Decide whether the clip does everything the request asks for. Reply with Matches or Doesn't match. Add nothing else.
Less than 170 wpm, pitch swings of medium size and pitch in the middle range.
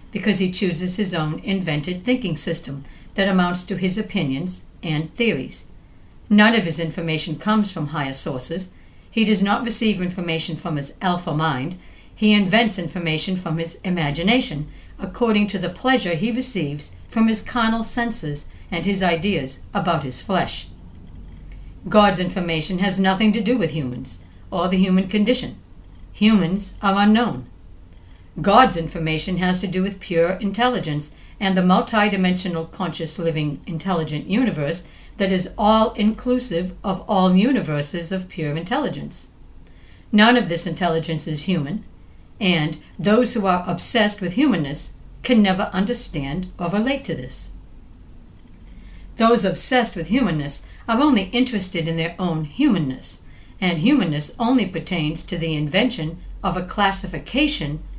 Matches